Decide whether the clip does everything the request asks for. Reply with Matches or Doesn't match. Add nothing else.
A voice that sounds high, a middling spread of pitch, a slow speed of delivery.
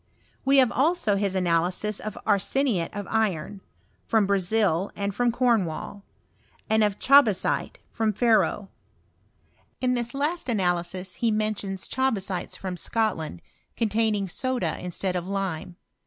Matches